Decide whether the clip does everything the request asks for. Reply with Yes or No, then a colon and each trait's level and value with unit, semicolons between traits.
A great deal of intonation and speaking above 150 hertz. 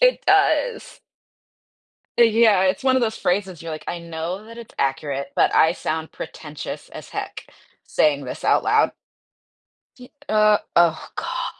Yes: wide, 6.3 semitones; medium, 185 Hz